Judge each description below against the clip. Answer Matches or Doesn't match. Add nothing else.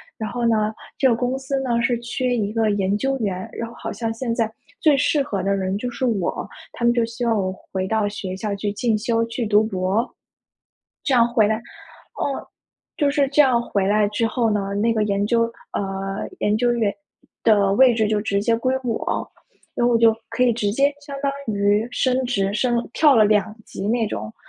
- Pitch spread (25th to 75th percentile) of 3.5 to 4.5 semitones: Doesn't match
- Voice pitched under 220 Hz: Doesn't match